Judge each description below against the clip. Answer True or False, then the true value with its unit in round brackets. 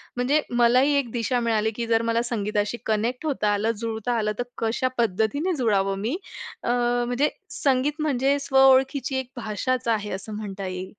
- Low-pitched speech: False (235 Hz)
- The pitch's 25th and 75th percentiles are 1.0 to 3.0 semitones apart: False (3.6 semitones)